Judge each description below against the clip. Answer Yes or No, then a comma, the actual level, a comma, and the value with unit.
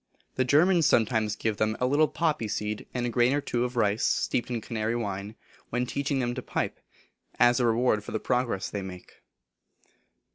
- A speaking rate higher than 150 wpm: Yes, average, 190 wpm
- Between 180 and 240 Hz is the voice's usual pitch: No, low, 120 Hz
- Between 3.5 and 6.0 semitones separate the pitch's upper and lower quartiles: No, average, 2.9 semitones